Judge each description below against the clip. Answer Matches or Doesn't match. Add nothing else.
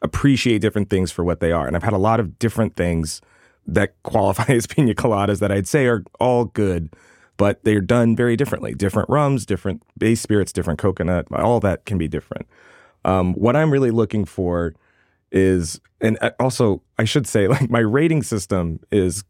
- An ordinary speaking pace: Matches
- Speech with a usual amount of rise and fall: Matches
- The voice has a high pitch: Doesn't match